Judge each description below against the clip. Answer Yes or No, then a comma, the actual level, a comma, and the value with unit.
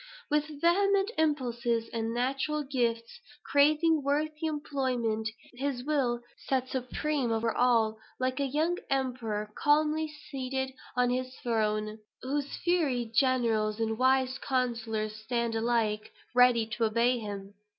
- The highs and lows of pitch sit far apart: No, average, 3.8 semitones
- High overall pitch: Yes, very high, 255 Hz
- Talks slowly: Yes, slow, 120 wpm